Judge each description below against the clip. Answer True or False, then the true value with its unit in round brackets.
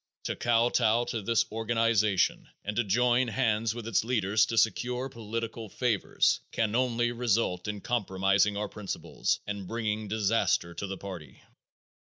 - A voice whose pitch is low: True (110 Hz)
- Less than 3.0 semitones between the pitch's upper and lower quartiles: True (2.5 semitones)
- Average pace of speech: True (145 wpm)